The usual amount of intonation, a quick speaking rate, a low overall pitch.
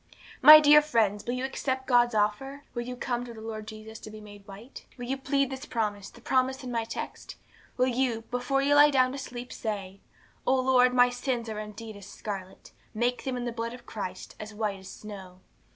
No: average, 3.3 semitones; fast, 215 wpm; high, 240 Hz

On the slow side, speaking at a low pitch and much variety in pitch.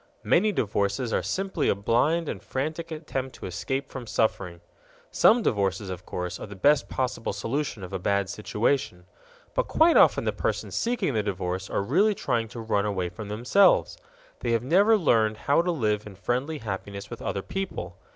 No: average, 180 wpm; low, 115 Hz; wide, 7.4 semitones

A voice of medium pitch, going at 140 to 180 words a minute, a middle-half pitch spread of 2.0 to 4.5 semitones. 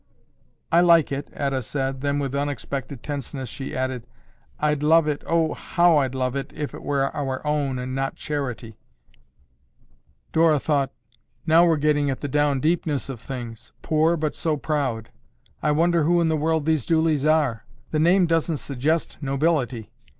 Yes: medium, 145 Hz; average, 165 wpm; average, 3.0 semitones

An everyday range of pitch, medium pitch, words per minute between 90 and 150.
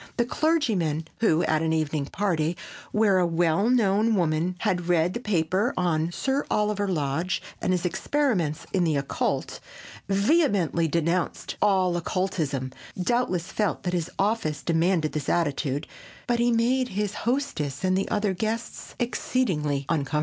Yes: average, 4.9 semitones; medium, 180 Hz; average, 145 wpm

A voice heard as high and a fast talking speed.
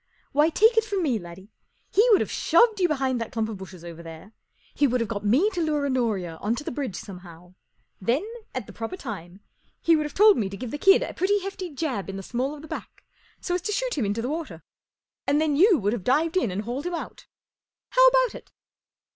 Yes: very high, 270 Hz; fast, 240 wpm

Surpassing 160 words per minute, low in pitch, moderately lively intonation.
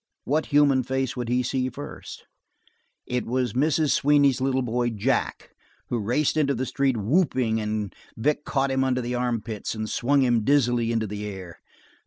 Yes: average, 170 wpm; low, 125 Hz; average, 3.2 semitones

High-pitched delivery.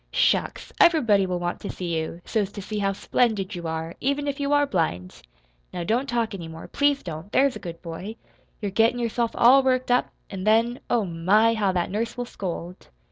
Yes: high, 210 Hz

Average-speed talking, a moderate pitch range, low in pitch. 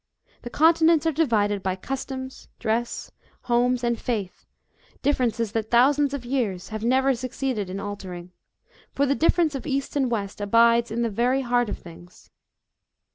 No: average, 160 wpm; average, 4.2 semitones; high, 240 Hz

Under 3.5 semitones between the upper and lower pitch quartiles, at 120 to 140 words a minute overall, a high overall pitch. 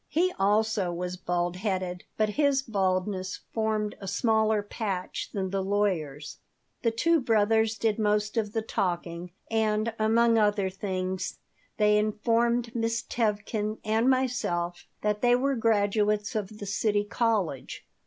Yes: average, 2.9 semitones; slow, 135 wpm; high, 210 Hz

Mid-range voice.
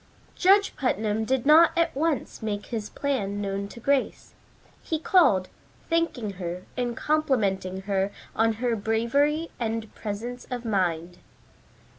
No: high, 225 Hz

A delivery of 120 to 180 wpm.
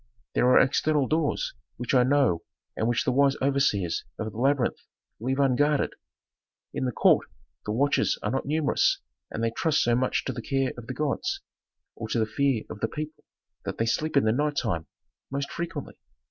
No: average, 190 wpm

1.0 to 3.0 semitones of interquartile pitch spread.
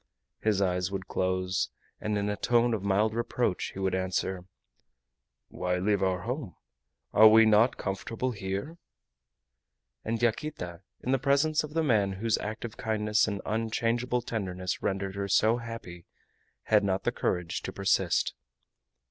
No: average, 3.4 semitones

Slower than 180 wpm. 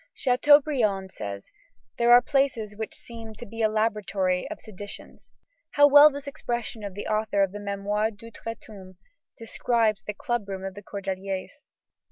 Yes: average, 160 wpm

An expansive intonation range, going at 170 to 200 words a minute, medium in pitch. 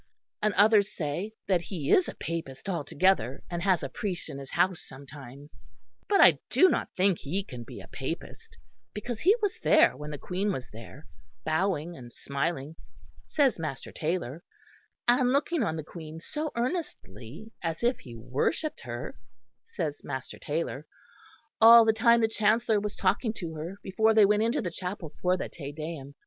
Yes: wide, 6.9 semitones; average, 175 wpm; medium, 175 Hz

